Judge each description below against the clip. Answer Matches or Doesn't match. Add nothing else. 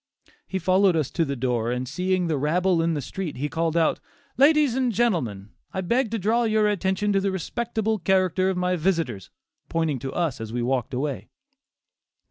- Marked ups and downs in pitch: Matches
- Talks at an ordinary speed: Matches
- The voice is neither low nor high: Matches